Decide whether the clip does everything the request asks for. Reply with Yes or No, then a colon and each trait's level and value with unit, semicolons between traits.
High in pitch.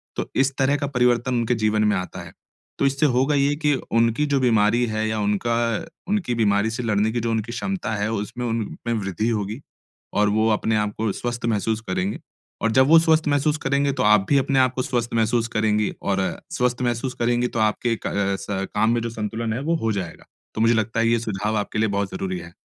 No: low, 115 Hz